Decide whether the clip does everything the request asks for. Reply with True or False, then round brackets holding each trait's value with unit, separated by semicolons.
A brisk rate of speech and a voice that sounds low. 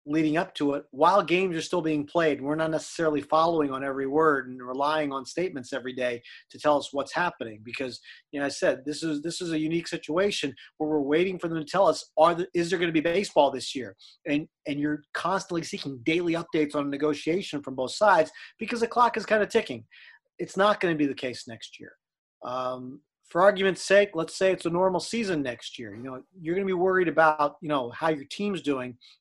False (230 wpm; 155 Hz)